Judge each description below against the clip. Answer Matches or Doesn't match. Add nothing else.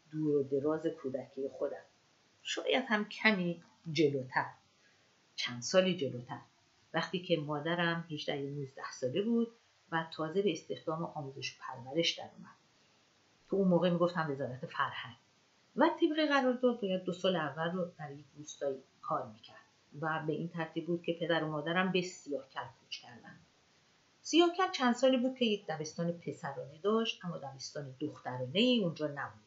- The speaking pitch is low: Doesn't match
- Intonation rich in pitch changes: Doesn't match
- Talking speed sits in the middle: Doesn't match